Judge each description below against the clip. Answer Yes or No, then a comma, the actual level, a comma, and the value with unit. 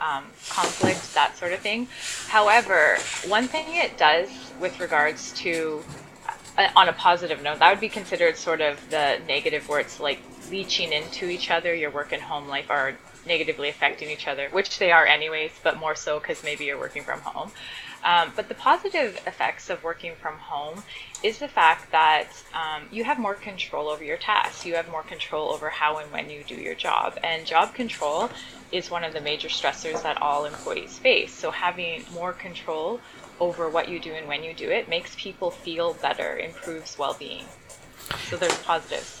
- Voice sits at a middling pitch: Yes, medium, 170 Hz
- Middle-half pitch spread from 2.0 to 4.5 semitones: No, average, 5.0 semitones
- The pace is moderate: Yes, average, 190 wpm